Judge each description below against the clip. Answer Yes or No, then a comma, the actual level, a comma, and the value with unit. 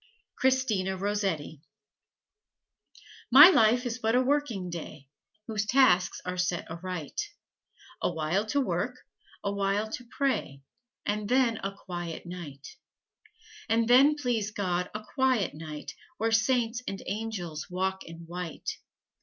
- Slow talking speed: Yes, slow, 130 wpm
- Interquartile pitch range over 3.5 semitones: Yes, wide, 5.4 semitones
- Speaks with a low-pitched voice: No, high, 200 Hz